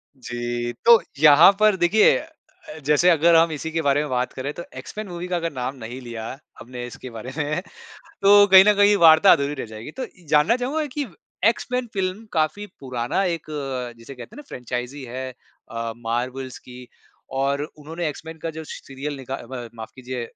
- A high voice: No, medium, 145 Hz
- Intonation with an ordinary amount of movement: No, wide, 5.9 semitones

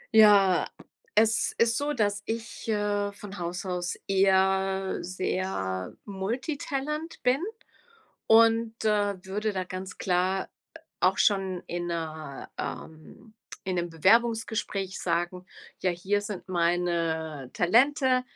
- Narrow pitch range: No, average, 3.8 semitones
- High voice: Yes, high, 195 Hz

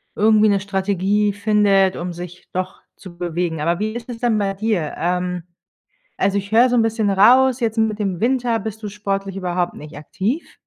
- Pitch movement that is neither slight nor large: Yes, average, 3.3 semitones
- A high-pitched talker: Yes, high, 200 Hz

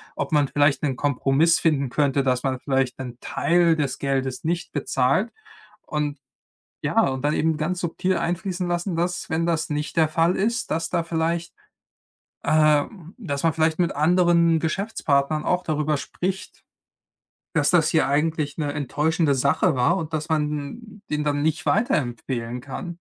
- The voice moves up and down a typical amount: Yes, average, 3.1 semitones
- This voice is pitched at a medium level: Yes, medium, 155 Hz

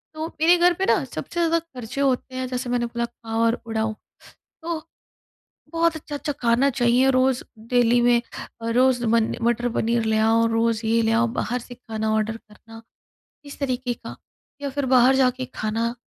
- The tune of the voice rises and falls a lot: No, narrow, 2.6 semitones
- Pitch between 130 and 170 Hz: No, high, 245 Hz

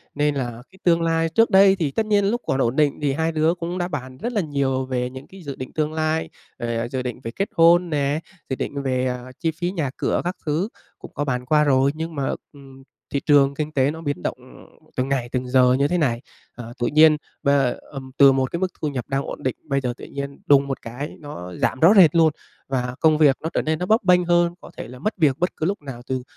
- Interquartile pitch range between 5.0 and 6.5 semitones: No, average, 3.9 semitones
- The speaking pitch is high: No, medium, 145 Hz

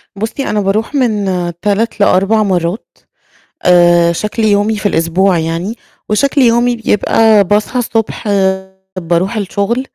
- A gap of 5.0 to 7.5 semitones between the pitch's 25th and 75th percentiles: No, average, 3.5 semitones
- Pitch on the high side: Yes, high, 205 Hz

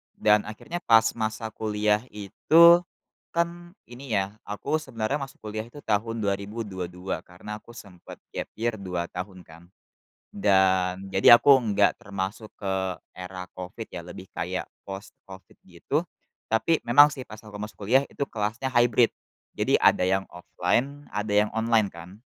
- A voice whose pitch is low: Yes, low, 105 Hz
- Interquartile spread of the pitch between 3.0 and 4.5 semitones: Yes, average, 3.6 semitones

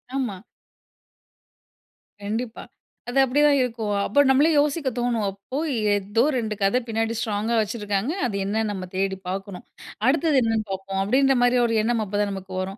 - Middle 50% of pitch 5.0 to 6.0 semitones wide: No, average, 3.9 semitones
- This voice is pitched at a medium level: No, high, 220 Hz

